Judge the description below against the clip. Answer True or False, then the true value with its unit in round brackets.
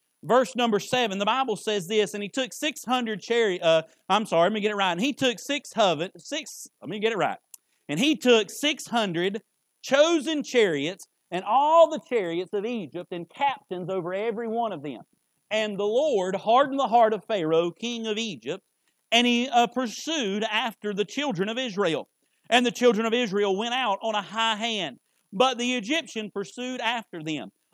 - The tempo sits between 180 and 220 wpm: True (190 wpm)